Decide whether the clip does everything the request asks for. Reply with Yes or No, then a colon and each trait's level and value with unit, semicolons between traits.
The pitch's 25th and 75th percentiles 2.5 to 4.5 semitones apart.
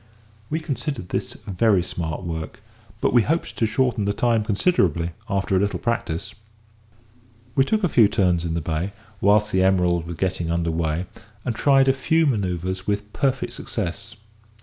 No: wide, 5.6 semitones